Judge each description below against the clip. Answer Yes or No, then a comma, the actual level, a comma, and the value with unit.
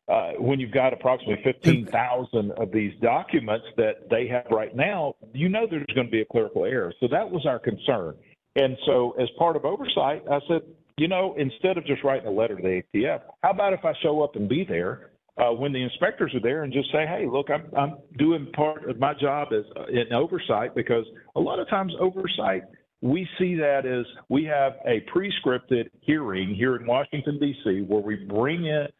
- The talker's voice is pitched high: No, medium, 140 Hz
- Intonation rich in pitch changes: No, average, 4.3 semitones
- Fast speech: Yes, fast, 210 wpm